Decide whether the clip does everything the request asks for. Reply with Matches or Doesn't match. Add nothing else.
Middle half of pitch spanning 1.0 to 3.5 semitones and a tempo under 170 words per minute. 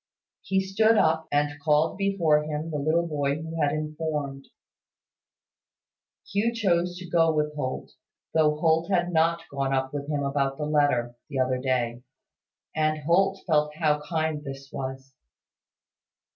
Matches